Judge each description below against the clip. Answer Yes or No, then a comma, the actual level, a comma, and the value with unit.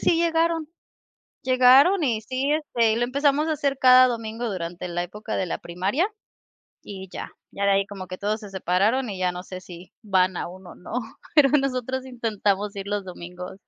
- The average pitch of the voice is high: Yes, high, 215 Hz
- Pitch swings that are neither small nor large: No, wide, 5.8 semitones